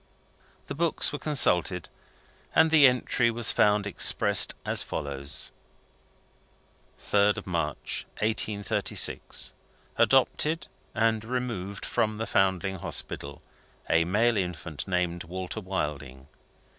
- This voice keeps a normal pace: No, slow, 100 wpm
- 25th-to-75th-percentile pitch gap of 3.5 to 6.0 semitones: Yes, average, 4.7 semitones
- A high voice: No, low, 100 Hz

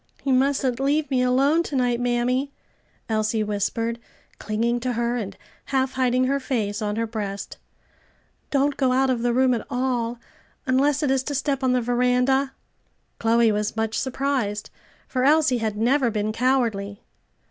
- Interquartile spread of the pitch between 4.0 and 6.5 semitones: No, average, 2.8 semitones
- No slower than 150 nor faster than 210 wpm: Yes, average, 160 wpm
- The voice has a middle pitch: No, very high, 250 Hz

